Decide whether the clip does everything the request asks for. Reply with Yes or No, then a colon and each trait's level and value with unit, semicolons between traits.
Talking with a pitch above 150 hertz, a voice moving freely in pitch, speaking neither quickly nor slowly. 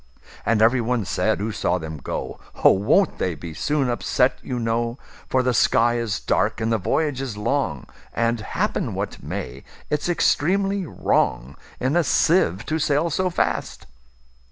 No: low, 120 Hz; wide, 5.7 semitones; average, 155 wpm